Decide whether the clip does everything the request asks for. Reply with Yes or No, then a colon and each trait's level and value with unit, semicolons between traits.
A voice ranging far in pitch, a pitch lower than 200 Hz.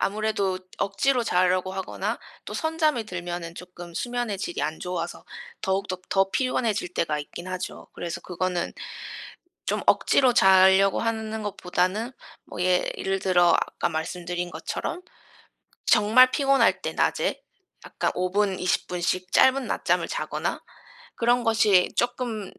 No: average, 4.2 semitones; high, 190 Hz